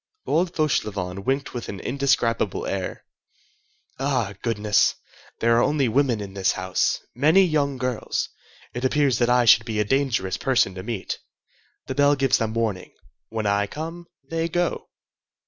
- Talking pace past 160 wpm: No, average, 150 wpm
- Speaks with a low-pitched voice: Yes, low, 125 Hz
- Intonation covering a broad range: No, average, 5.0 semitones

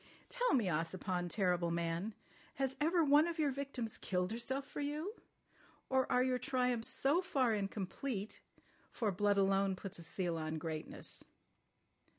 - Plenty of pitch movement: Yes, wide, 7.1 semitones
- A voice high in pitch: Yes, high, 220 Hz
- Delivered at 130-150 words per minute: Yes, average, 140 wpm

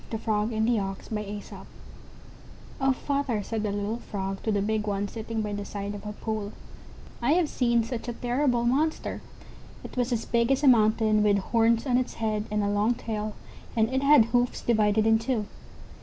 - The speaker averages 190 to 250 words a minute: Yes, average, 195 wpm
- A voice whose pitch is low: No, high, 225 Hz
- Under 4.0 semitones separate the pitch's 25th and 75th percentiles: Yes, narrow, 2.5 semitones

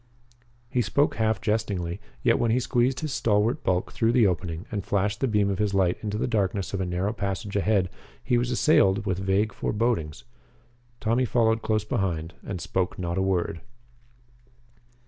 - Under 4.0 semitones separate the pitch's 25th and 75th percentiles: Yes, average, 3.2 semitones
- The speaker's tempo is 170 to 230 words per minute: Yes, average, 175 wpm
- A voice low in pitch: Yes, low, 105 Hz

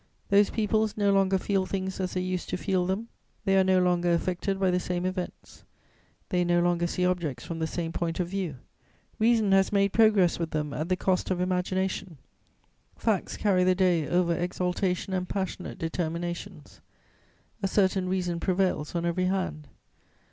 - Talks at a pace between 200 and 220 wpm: No, average, 175 wpm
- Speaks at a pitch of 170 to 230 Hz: Yes, medium, 185 Hz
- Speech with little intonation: Yes, narrow, 1.8 semitones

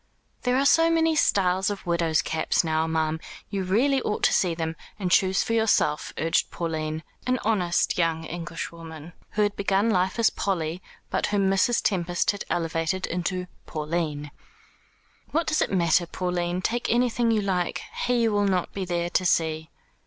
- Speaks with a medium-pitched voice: Yes, medium, 180 Hz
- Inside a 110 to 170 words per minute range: Yes, average, 165 wpm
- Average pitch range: Yes, average, 4.0 semitones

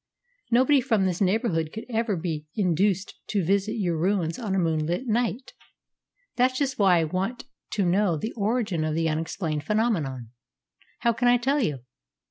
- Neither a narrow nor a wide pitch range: No, wide, 6.0 semitones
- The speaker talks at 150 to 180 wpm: Yes, average, 165 wpm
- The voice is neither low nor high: No, high, 195 Hz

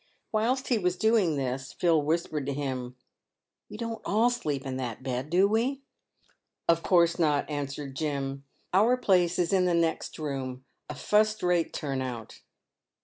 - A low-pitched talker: No, medium, 165 Hz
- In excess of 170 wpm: Yes, average, 180 wpm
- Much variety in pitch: Yes, wide, 6.6 semitones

